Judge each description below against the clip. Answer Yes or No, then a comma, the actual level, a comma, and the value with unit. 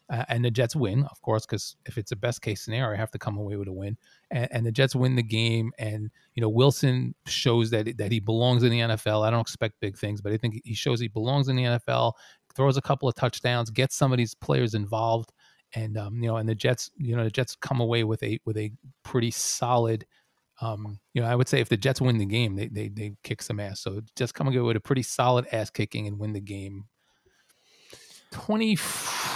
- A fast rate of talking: Yes, fast, 245 wpm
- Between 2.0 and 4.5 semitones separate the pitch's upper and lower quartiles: Yes, narrow, 2.6 semitones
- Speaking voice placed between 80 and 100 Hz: No, low, 115 Hz